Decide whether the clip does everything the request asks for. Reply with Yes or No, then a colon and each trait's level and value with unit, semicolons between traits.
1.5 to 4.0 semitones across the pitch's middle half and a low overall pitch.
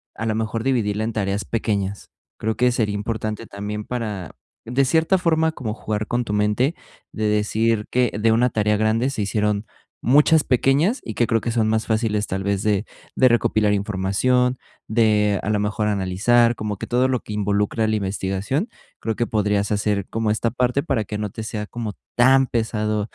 Yes: narrow, 2.5 semitones; low, 110 Hz